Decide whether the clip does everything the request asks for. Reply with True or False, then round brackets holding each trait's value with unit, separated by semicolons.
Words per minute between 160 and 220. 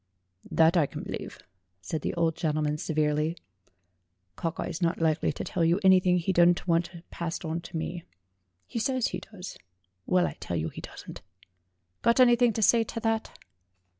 True (175 wpm)